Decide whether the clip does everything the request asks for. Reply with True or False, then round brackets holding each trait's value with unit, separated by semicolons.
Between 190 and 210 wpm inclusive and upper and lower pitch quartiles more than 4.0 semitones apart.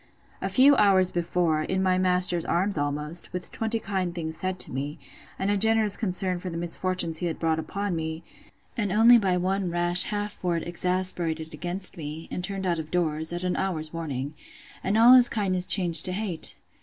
False (195 wpm; 2.9 semitones)